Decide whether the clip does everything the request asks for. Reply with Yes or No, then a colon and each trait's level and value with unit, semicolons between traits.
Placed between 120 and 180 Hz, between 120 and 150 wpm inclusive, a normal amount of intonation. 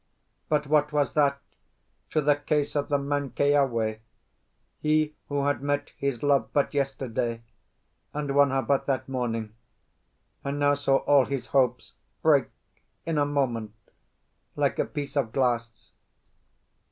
No: medium, 140 Hz; average, 140 wpm; narrow, 2.1 semitones